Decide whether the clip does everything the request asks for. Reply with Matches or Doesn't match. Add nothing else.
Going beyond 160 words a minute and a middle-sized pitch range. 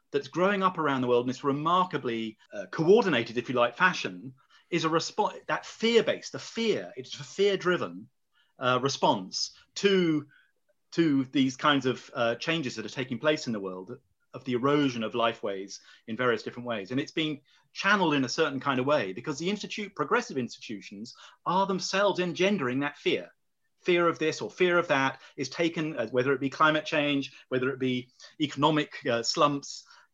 Doesn't match